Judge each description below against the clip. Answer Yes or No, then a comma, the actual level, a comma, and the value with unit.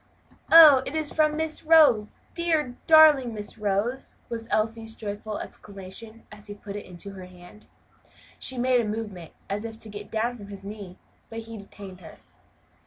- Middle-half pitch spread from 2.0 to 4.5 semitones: Yes, average, 3.9 semitones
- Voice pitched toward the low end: No, high, 220 Hz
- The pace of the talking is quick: No, average, 175 wpm